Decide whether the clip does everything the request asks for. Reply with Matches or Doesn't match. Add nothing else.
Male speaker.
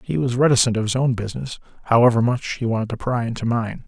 Matches